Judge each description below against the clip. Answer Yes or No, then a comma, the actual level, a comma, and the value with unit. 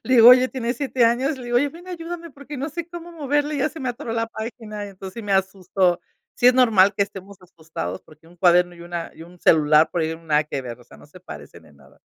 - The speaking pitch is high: Yes, high, 210 Hz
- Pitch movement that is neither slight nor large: No, wide, 7.2 semitones